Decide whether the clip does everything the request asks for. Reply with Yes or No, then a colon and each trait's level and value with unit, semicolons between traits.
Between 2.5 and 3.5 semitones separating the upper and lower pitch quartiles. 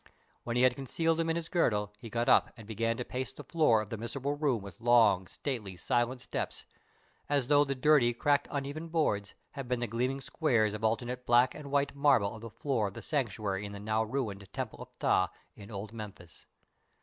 No: average, 4.7 semitones